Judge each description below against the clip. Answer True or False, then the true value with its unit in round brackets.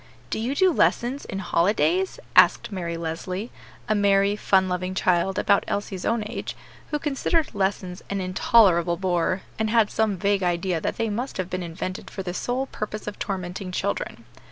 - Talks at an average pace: True (175 wpm)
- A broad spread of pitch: False (3.2 semitones)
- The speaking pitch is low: False (195 Hz)